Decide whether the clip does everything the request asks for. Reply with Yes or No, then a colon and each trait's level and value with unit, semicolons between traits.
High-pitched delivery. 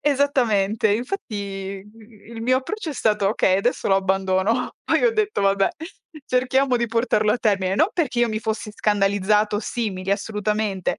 Yes: high, 215 Hz